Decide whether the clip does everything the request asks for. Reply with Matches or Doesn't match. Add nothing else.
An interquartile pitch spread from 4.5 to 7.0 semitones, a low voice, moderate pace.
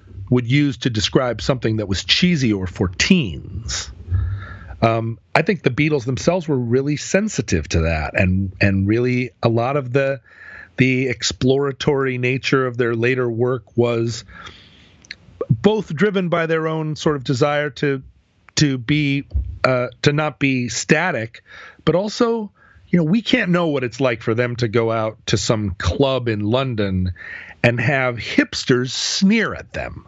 Matches